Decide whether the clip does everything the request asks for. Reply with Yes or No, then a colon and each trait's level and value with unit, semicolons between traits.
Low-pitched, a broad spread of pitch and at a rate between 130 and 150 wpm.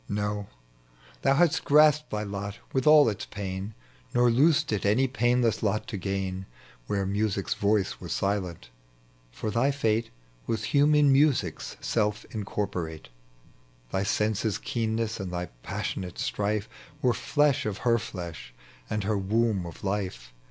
No: low, 105 Hz; average, 3.7 semitones; average, 140 wpm